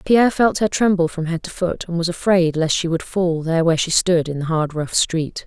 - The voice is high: No, medium, 170 Hz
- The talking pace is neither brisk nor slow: No, fast, 265 wpm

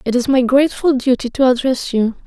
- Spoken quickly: Yes, fast, 210 wpm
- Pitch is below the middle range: No, very high, 255 Hz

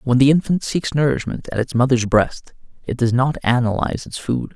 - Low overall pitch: Yes, low, 130 Hz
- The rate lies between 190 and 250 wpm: Yes, average, 200 wpm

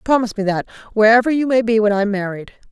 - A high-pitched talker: Yes, high, 220 Hz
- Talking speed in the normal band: No, fast, 220 wpm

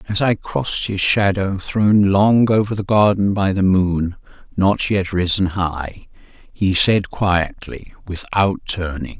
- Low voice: Yes, very low, 95 Hz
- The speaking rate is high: No, average, 145 wpm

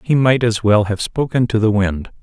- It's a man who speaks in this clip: Yes, male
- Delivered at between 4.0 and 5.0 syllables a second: Yes, 4.9 syllables/s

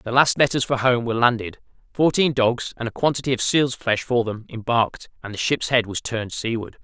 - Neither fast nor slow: No, fast, 220 wpm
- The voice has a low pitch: Yes, low, 120 Hz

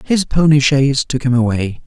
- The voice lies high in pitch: No, low, 135 Hz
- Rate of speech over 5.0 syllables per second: Yes, 5.2 syllables/s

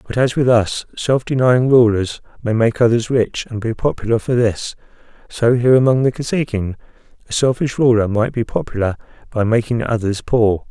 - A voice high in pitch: No, low, 115 Hz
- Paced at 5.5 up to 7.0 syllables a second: No, 5.2 syllables/s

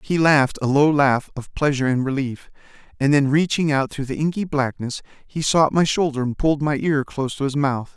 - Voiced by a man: Yes, male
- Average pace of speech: No, fast, 220 wpm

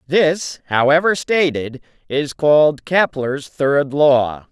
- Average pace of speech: No, slow, 105 wpm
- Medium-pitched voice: Yes, medium, 145 Hz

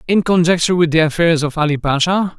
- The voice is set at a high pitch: No, medium, 165 Hz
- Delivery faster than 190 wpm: Yes, average, 200 wpm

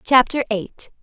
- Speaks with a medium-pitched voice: No, high, 240 Hz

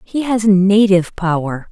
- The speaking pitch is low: No, high, 195 Hz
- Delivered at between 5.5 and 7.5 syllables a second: No, 4.4 syllables/s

